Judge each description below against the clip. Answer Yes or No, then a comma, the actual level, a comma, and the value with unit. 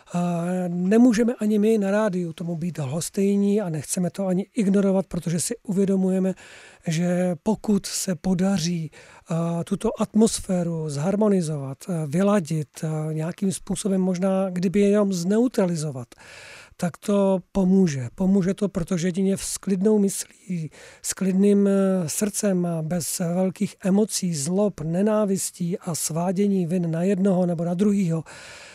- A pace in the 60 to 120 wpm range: Yes, slow, 115 wpm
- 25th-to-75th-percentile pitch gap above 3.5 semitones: No, narrow, 2.6 semitones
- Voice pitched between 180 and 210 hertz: Yes, high, 190 Hz